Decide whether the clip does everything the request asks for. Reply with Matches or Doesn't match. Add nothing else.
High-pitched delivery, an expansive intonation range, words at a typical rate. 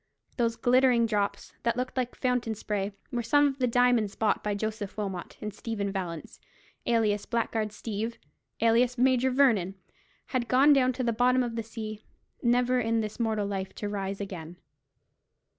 Doesn't match